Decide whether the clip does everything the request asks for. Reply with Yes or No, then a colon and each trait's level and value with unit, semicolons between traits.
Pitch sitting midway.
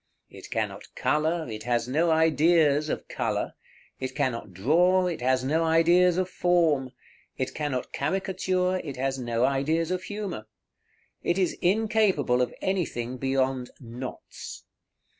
Yes: medium, 155 Hz